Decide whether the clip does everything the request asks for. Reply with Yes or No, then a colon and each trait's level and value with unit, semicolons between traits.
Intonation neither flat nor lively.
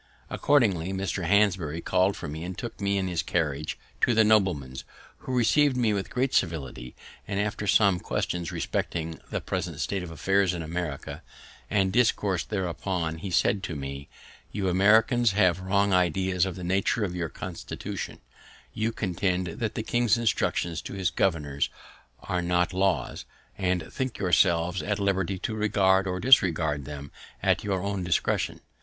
Yes: average, 3.0 semitones